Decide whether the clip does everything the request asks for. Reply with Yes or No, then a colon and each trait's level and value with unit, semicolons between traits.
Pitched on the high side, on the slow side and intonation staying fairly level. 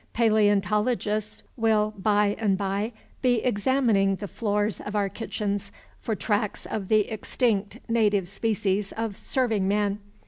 Yes: high, 210 Hz; slow, 130 wpm; narrow, 1.8 semitones